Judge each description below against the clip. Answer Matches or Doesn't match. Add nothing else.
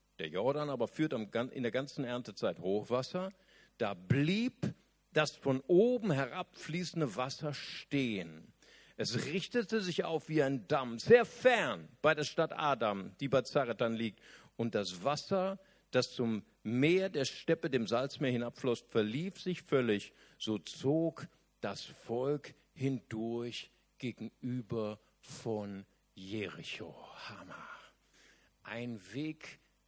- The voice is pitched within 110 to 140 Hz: Matches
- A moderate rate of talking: Doesn't match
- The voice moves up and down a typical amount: Doesn't match